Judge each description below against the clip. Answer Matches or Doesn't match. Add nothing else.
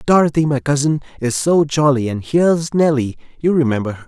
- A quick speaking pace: Doesn't match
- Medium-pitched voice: Matches